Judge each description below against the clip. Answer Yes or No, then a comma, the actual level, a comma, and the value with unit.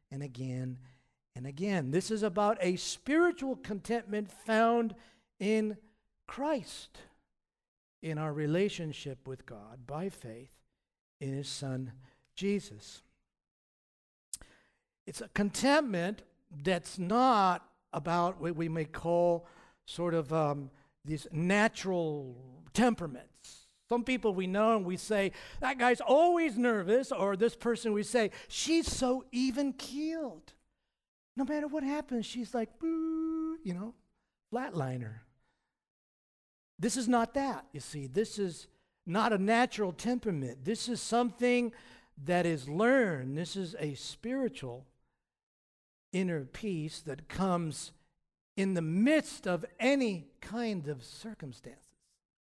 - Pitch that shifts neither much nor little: No, wide, 7.7 semitones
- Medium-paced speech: No, slow, 120 wpm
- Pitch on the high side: Yes, high, 195 Hz